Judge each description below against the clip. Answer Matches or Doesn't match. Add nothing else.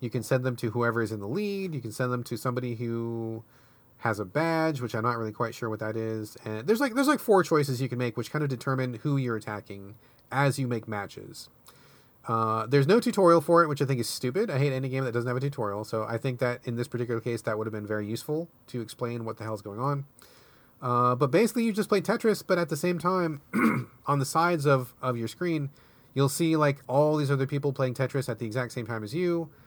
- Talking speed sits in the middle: Doesn't match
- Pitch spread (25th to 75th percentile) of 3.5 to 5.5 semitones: Matches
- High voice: Doesn't match